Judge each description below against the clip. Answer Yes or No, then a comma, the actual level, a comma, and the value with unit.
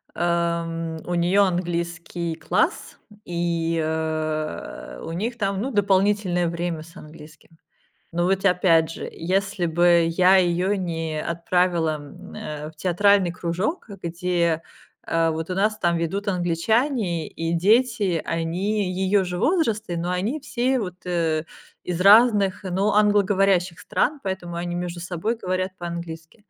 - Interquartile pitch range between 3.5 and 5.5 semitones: No, average, 2.9 semitones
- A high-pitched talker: No, medium, 175 Hz